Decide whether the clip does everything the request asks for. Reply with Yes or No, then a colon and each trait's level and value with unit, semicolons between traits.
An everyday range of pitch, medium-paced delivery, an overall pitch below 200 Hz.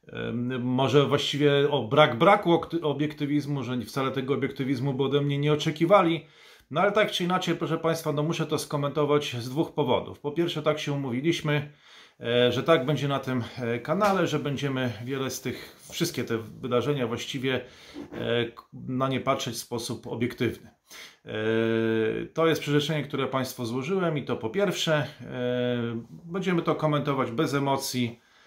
Yes: average, 3.8 semitones; average, 150 wpm; medium, 140 Hz